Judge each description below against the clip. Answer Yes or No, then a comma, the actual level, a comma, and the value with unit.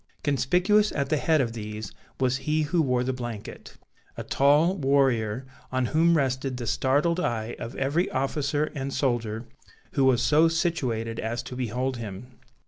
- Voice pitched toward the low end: Yes, low, 130 Hz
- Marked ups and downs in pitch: No, average, 4.1 semitones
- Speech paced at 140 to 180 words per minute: Yes, average, 160 wpm